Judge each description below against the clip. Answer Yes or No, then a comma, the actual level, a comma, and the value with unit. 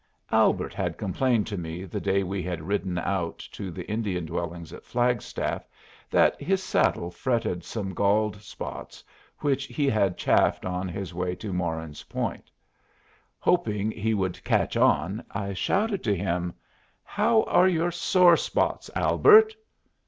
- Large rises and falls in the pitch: Yes, wide, 5.7 semitones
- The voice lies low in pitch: Yes, low, 100 Hz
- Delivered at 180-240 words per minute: No, average, 145 wpm